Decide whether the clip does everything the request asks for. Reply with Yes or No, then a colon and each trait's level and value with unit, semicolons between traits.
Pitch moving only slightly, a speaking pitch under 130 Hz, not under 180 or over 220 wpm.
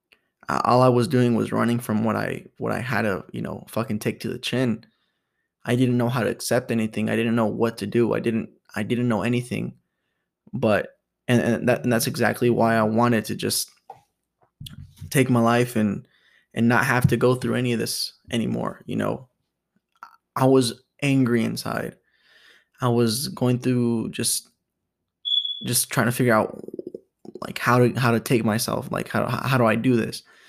Yes: narrow, 1.5 semitones; low, 120 Hz; average, 185 wpm